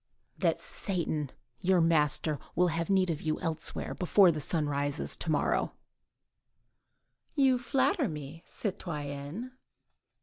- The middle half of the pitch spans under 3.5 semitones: No, average, 4.2 semitones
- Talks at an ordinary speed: No, slow, 115 wpm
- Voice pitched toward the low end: No, medium, 165 Hz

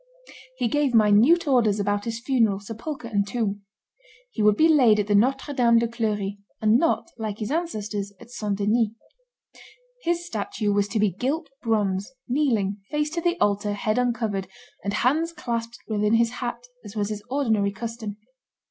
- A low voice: No, high, 225 Hz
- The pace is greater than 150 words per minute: Yes, average, 165 wpm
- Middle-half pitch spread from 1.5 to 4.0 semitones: Yes, average, 3.6 semitones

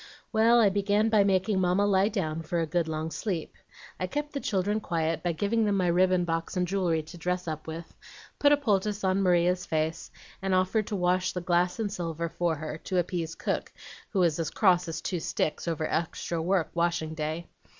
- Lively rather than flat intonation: No, average, 3.1 semitones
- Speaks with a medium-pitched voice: Yes, medium, 180 Hz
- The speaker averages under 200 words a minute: No, fast, 205 wpm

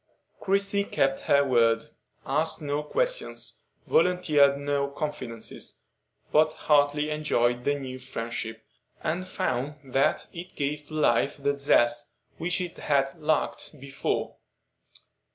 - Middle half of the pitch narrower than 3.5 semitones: Yes, average, 3.1 semitones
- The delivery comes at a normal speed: No, slow, 115 wpm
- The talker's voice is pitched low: No, medium, 145 Hz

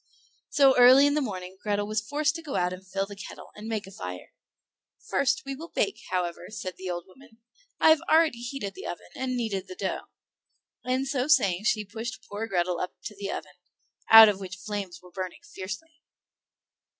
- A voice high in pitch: Yes, high, 210 Hz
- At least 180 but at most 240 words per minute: Yes, average, 200 wpm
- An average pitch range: No, wide, 5.8 semitones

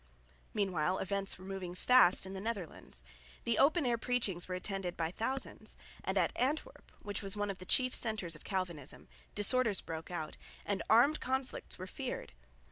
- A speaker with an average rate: Yes, average, 170 wpm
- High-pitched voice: Yes, high, 195 Hz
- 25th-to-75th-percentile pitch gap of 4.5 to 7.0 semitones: Yes, average, 5.1 semitones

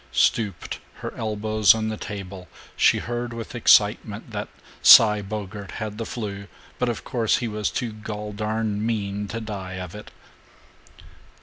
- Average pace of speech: Yes, average, 150 wpm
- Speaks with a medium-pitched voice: No, low, 105 Hz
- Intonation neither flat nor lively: No, narrow, 1.7 semitones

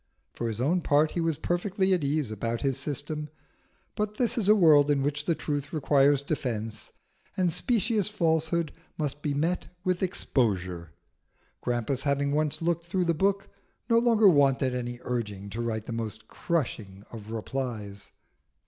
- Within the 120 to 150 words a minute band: No, average, 160 wpm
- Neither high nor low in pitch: Yes, medium, 145 Hz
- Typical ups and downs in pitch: No, wide, 6.3 semitones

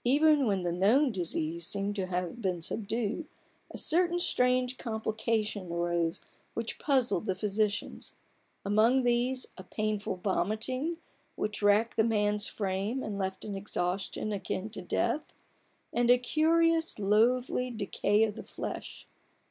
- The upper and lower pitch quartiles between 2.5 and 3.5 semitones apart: No, average, 4.3 semitones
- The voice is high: Yes, high, 215 Hz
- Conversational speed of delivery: No, slow, 130 wpm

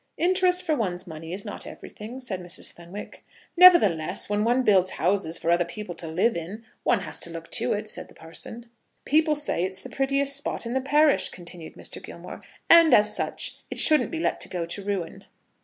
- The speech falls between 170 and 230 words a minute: Yes, average, 200 wpm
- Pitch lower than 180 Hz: No, high, 210 Hz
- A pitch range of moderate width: No, wide, 7.9 semitones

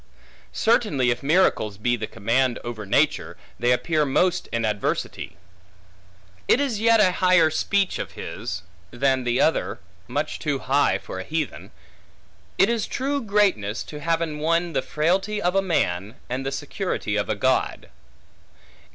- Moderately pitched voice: Yes, medium, 150 Hz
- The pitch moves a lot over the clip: Yes, wide, 7.5 semitones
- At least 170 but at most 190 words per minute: No, average, 155 wpm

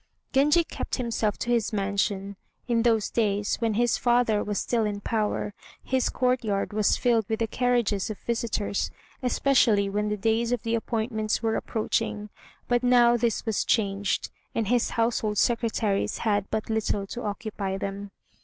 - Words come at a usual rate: Yes, average, 160 wpm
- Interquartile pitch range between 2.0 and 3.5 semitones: Yes, narrow, 2.5 semitones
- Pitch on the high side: Yes, high, 220 Hz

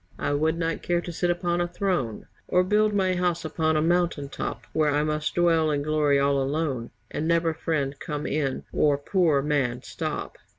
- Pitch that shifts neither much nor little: Yes, average, 3.3 semitones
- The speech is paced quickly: No, average, 195 wpm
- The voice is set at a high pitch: No, medium, 155 Hz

